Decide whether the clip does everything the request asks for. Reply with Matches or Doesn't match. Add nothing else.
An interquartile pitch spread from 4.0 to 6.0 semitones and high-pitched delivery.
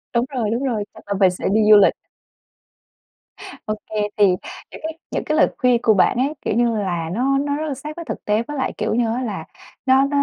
Matches